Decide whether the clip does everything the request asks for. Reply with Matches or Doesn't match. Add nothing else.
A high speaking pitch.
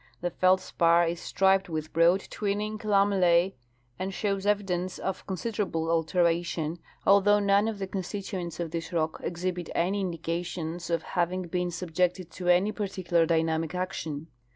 Doesn't match